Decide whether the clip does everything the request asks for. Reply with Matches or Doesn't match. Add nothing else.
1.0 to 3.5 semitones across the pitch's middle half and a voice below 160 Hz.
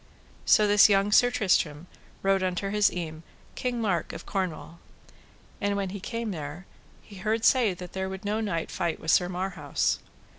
Doesn't match